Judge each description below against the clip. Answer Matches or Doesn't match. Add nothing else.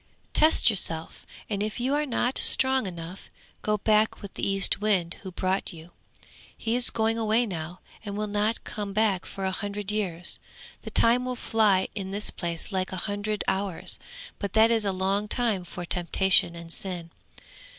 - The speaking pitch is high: Matches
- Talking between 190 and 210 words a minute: Doesn't match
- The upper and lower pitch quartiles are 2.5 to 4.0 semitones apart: Matches